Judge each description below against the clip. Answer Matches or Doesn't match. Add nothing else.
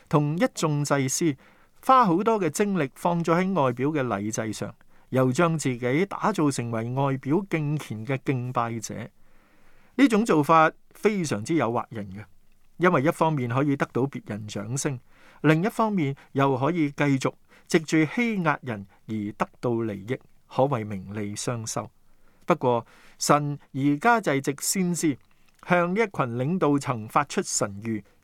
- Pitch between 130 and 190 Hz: Matches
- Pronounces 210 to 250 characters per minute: Matches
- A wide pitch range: Matches